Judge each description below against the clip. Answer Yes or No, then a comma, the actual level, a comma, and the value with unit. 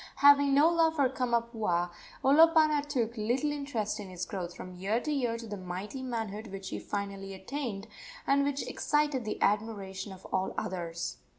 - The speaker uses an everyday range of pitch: No, wide, 6.4 semitones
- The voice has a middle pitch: No, high, 225 Hz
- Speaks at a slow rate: No, average, 170 wpm